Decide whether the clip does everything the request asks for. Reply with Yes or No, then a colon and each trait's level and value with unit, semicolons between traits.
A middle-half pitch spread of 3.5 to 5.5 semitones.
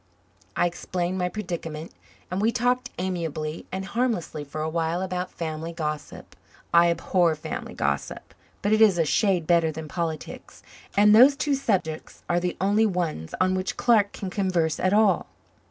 Yes: average, 3.8 semitones